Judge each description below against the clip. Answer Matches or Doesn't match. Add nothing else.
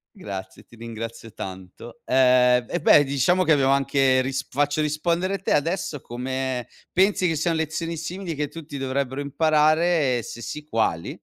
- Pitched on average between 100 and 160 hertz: Matches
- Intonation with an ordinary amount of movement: Matches